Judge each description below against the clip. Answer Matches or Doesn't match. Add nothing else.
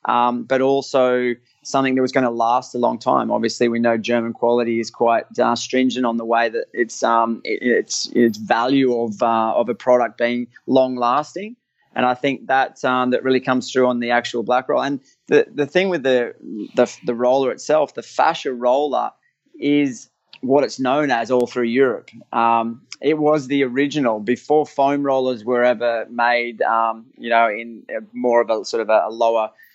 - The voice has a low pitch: Matches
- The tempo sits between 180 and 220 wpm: Matches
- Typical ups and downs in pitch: Doesn't match